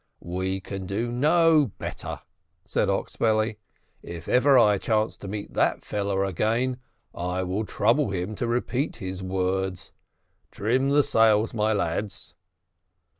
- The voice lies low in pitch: Yes, low, 105 Hz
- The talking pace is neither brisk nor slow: No, slow, 130 wpm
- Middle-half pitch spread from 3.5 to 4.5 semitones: Yes, average, 4.1 semitones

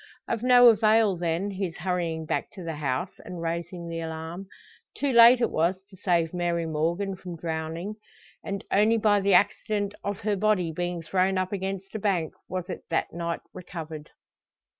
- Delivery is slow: No, average, 175 wpm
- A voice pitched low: No, medium, 180 Hz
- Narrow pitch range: No, average, 3.3 semitones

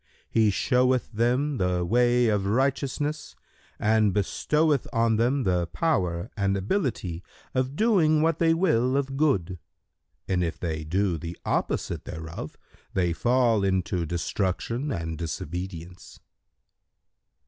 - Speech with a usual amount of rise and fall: No, wide, 7.0 semitones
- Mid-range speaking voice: No, low, 110 Hz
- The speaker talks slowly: Yes, slow, 120 wpm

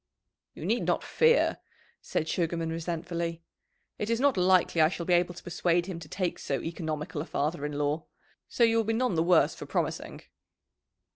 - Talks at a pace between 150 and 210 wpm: Yes, average, 190 wpm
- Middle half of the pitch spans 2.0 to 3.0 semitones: Yes, narrow, 2.4 semitones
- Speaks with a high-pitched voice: No, medium, 170 Hz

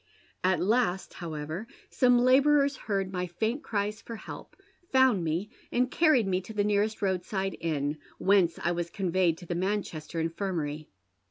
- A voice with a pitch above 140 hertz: Yes, high, 190 Hz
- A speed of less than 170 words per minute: Yes, average, 155 wpm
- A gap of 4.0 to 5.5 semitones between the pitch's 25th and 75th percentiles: Yes, average, 4.4 semitones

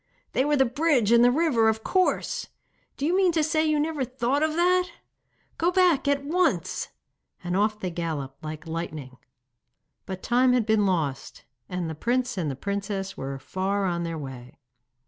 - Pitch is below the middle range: No, high, 220 Hz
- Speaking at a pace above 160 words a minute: Yes, average, 175 wpm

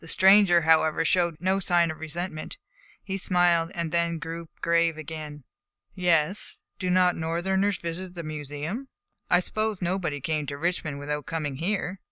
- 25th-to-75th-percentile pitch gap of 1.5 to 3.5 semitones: Yes, narrow, 2.6 semitones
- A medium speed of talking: Yes, average, 150 wpm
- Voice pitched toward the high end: No, medium, 170 Hz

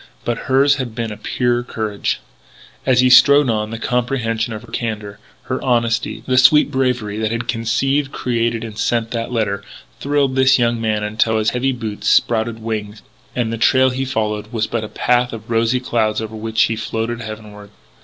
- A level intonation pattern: Yes, narrow, 2.2 semitones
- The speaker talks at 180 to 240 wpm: Yes, average, 185 wpm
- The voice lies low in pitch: Yes, low, 115 Hz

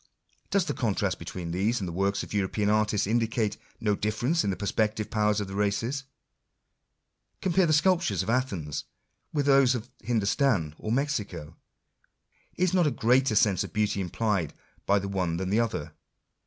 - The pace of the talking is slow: No, average, 170 wpm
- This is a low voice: Yes, low, 105 Hz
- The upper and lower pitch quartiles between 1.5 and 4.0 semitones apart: No, average, 4.5 semitones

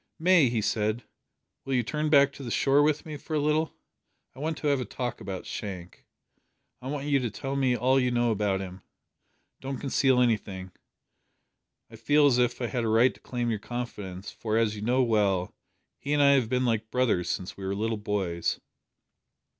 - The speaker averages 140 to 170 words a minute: No, average, 200 wpm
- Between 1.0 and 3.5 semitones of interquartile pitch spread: No, average, 4.7 semitones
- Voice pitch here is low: Yes, low, 120 Hz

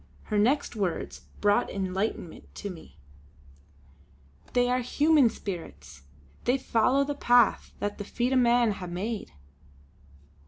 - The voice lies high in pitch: Yes, high, 220 Hz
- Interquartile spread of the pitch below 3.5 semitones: No, average, 4.5 semitones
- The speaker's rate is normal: No, slow, 125 wpm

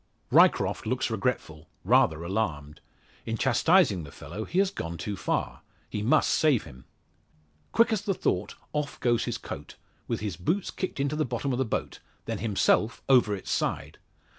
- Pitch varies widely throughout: Yes, wide, 8.2 semitones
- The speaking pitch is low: Yes, low, 115 Hz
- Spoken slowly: No, average, 170 wpm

